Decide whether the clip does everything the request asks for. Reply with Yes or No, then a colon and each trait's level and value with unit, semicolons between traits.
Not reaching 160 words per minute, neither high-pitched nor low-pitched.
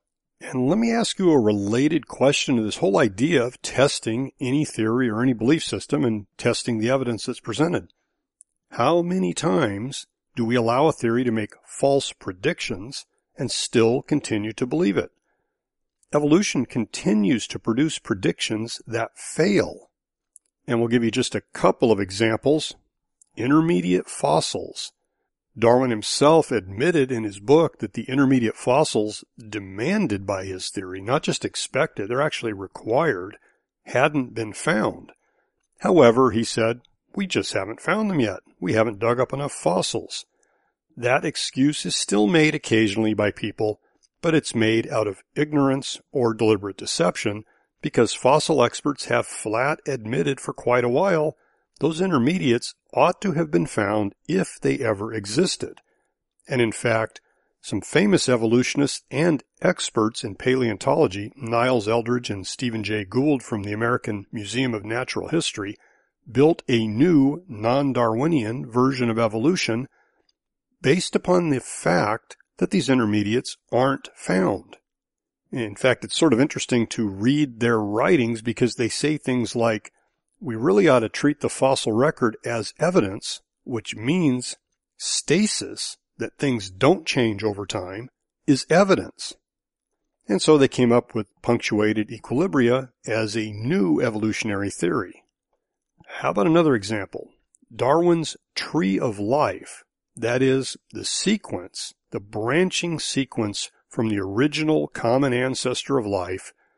No: average, 140 wpm; low, 120 Hz